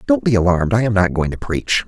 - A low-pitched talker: Yes, low, 100 Hz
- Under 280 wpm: No, fast, 290 wpm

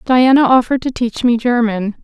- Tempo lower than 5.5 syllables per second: Yes, 5.3 syllables/s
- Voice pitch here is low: No, high, 240 Hz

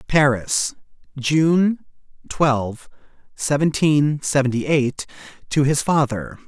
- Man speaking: Yes, male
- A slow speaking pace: Yes, slow, 85 wpm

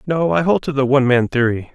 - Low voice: Yes, low, 130 Hz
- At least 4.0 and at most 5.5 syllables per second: No, 6.1 syllables/s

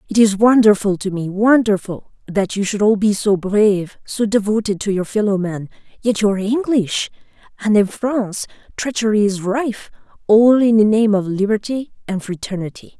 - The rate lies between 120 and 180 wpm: Yes, average, 150 wpm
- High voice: Yes, high, 210 Hz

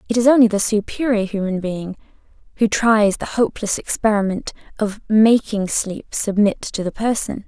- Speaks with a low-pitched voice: No, high, 210 Hz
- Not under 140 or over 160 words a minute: Yes, average, 155 wpm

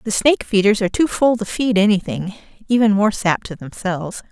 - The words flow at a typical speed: Yes, average, 180 wpm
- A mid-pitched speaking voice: No, high, 205 Hz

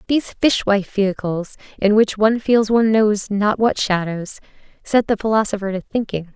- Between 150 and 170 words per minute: Yes, average, 160 wpm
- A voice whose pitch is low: No, high, 210 Hz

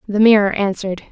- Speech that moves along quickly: No, average, 160 wpm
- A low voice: No, high, 205 Hz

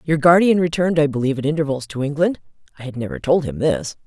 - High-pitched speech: No, medium, 145 Hz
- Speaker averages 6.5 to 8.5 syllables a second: Yes, 6.8 syllables/s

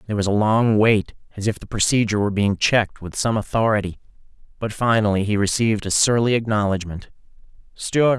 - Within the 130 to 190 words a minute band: Yes, average, 170 wpm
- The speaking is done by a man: Yes, male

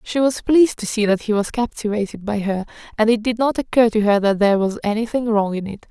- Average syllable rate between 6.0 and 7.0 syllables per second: Yes, 6.1 syllables/s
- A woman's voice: Yes, female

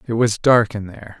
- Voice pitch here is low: Yes, low, 110 Hz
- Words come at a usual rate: No, fast, 250 wpm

